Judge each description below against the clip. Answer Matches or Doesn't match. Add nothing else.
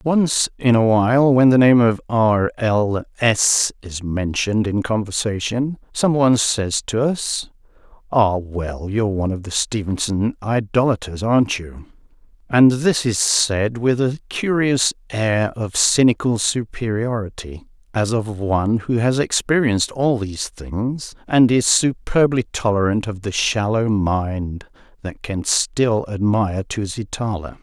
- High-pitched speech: Doesn't match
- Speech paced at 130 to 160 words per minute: Matches